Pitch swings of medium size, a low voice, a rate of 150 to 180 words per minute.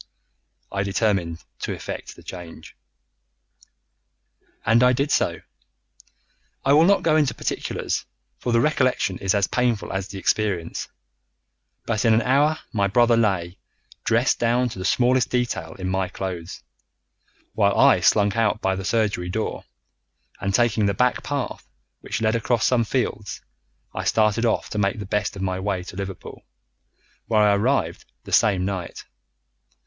Yes: average, 3.9 semitones; low, 105 Hz; average, 155 wpm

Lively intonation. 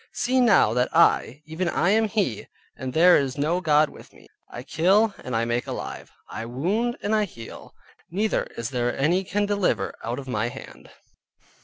Yes: wide, 8.4 semitones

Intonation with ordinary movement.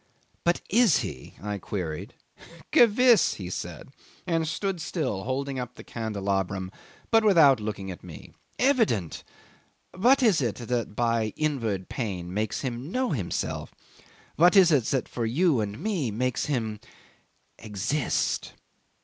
No: wide, 8.7 semitones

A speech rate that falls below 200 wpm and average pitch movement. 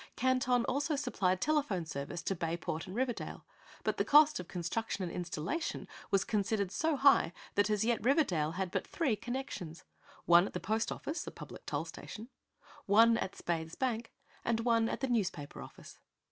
No: average, 175 wpm; wide, 6.3 semitones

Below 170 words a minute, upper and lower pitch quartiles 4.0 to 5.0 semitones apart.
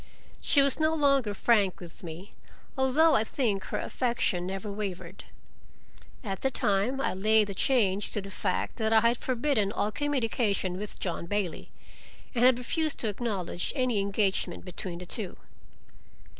Yes: average, 155 wpm; average, 4.7 semitones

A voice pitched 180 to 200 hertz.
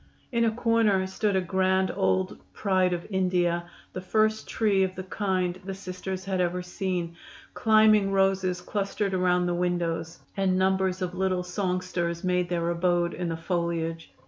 Yes: medium, 185 Hz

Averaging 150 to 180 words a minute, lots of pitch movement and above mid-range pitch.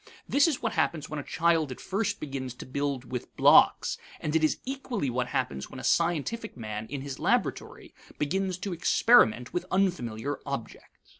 No: average, 175 wpm; wide, 6.5 semitones; medium, 150 Hz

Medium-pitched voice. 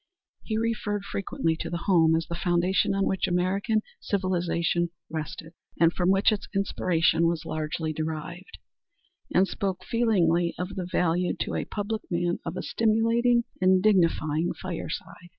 Yes: medium, 180 Hz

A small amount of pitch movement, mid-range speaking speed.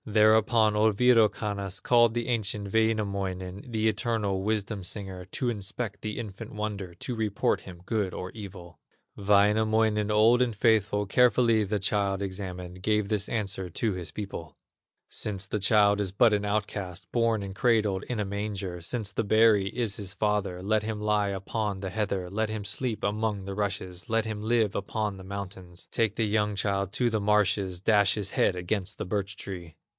Yes: narrow, 2.1 semitones; average, 175 wpm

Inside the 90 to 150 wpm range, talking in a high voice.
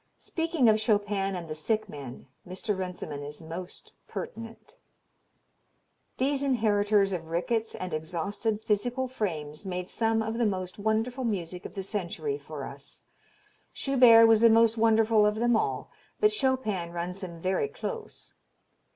Yes: average, 145 wpm; high, 210 Hz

